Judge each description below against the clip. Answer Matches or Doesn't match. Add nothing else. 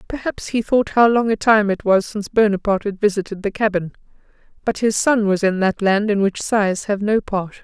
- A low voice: Doesn't match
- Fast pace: Matches